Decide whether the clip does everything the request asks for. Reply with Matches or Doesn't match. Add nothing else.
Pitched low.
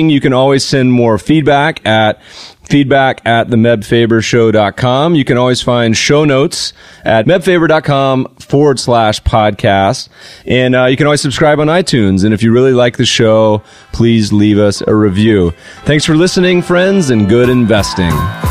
Matches